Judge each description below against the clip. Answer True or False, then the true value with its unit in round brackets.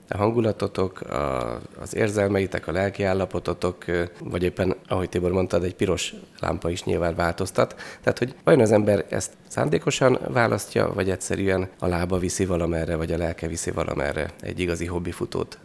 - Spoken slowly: False (155 wpm)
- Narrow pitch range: True (1.7 semitones)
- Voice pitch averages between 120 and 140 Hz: False (90 Hz)